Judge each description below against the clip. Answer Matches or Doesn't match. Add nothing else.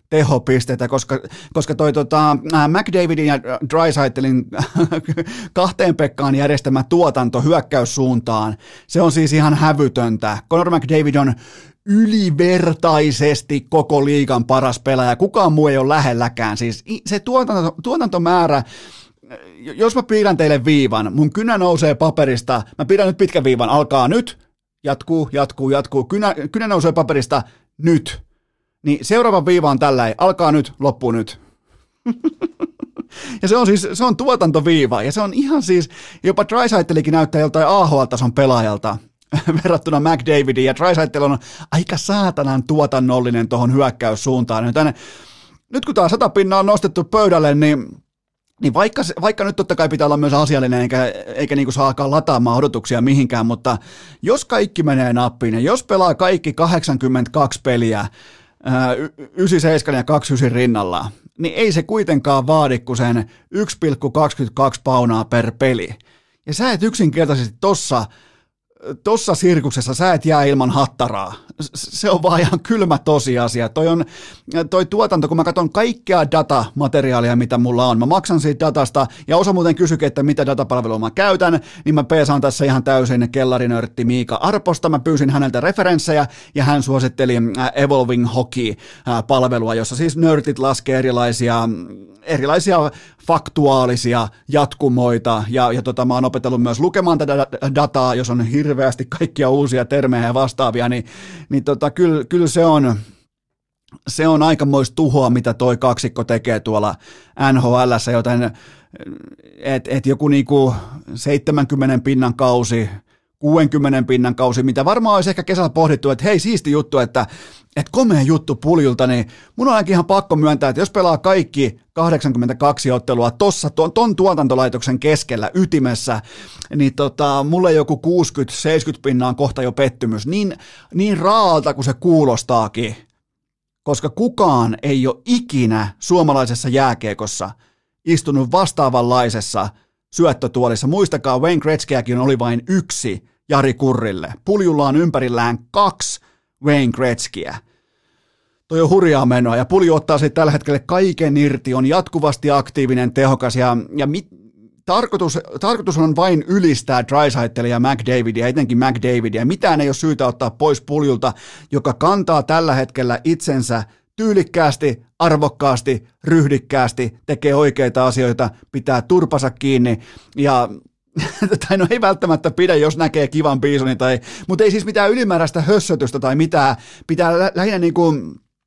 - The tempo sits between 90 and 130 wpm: Doesn't match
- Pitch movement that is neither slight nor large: Matches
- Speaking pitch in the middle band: Matches